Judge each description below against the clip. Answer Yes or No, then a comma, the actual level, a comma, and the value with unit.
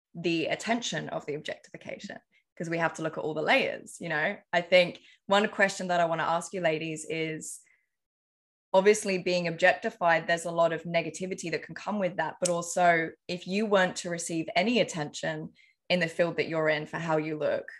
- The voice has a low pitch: No, medium, 170 Hz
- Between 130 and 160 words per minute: No, average, 200 wpm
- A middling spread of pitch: No, narrow, 2.3 semitones